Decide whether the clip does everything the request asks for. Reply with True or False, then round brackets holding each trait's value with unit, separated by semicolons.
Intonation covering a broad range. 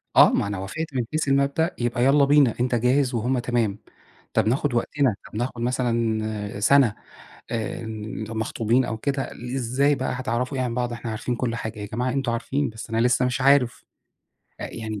False (3.0 semitones)